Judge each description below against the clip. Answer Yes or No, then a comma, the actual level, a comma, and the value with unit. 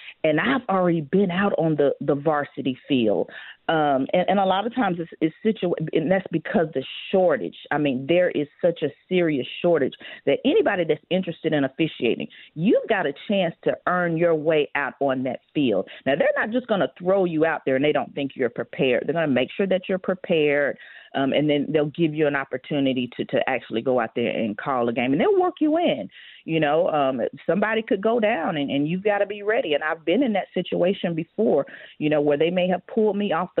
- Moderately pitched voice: Yes, medium, 165 Hz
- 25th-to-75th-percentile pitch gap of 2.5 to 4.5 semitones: No, average, 4.9 semitones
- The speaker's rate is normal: No, fast, 230 wpm